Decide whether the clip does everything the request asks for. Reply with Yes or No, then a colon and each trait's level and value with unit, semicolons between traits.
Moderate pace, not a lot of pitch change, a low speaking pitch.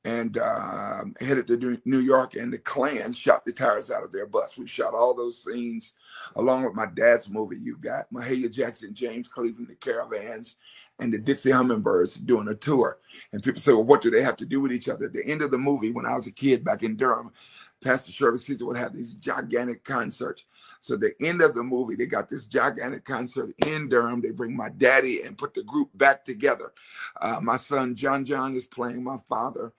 No: fast, 220 wpm; narrow, 2.3 semitones; low, 125 Hz